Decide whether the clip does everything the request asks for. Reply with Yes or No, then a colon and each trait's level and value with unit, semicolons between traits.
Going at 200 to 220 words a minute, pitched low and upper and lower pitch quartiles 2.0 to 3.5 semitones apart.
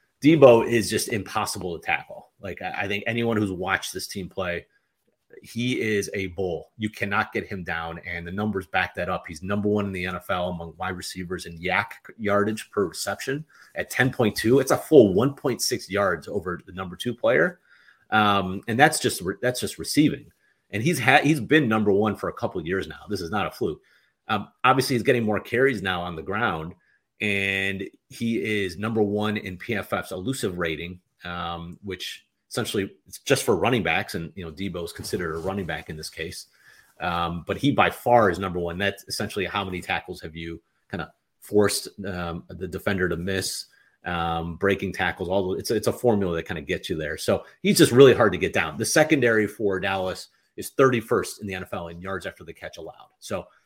Yes: fast, 205 wpm; very low, 95 Hz; average, 3.2 semitones